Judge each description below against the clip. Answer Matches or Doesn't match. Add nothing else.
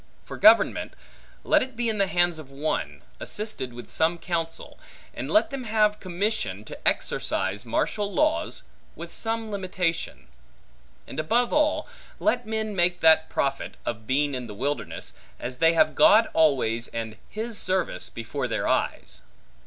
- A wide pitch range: Matches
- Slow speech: Doesn't match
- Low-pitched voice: Doesn't match